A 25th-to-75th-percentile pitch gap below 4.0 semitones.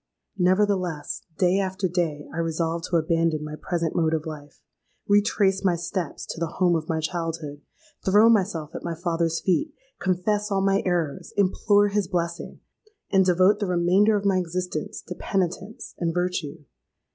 Yes: average, 3.0 semitones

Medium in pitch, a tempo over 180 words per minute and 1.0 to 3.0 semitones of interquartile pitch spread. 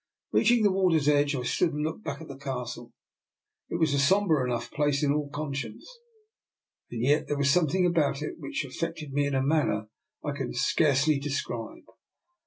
Yes: medium, 145 Hz; average, 190 wpm; average, 2.7 semitones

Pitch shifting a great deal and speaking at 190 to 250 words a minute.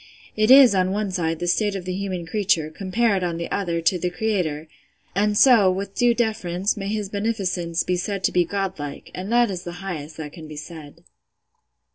No: average, 3.3 semitones; average, 200 wpm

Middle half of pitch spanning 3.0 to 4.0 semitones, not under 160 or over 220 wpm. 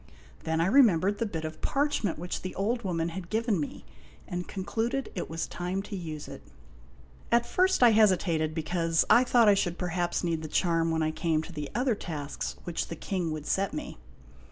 No: average, 4.7 semitones; average, 200 wpm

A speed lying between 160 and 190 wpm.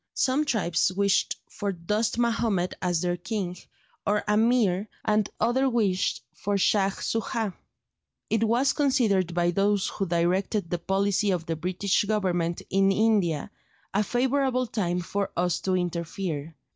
No: average, 140 wpm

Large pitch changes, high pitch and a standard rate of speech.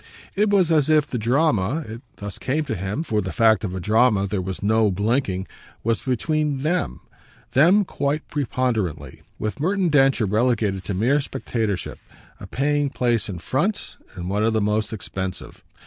No: wide, 6.2 semitones; low, 115 Hz; average, 170 wpm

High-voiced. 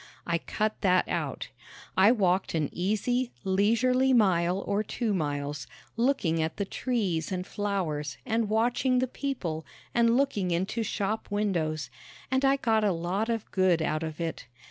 Yes: high, 200 Hz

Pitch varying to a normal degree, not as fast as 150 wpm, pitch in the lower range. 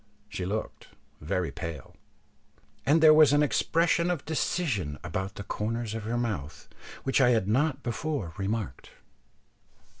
No: wide, 7.6 semitones; average, 140 wpm; low, 115 Hz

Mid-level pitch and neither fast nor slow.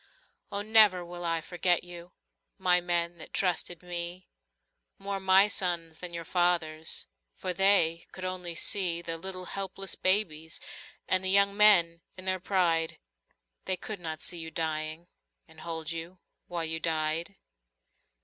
Yes: medium, 175 Hz; average, 150 wpm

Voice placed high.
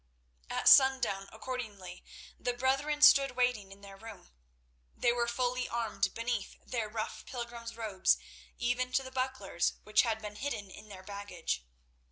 Yes: high, 230 Hz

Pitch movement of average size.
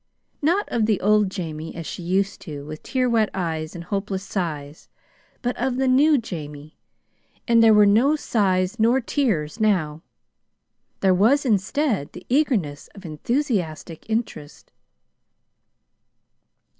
No: wide, 6.6 semitones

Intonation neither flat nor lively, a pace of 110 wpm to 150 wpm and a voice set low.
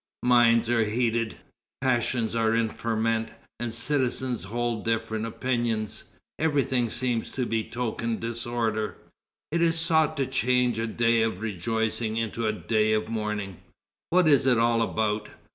No: narrow, 1.8 semitones; average, 140 wpm; low, 115 Hz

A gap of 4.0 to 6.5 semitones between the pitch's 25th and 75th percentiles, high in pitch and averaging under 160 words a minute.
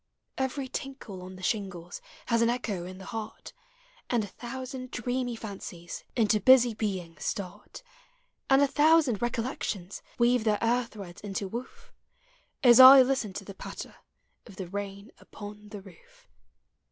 Yes: average, 4.4 semitones; high, 220 Hz; average, 150 wpm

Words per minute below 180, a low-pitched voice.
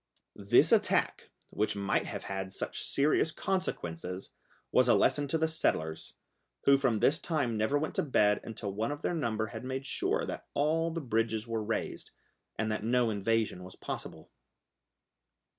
Yes: average, 165 wpm; low, 115 Hz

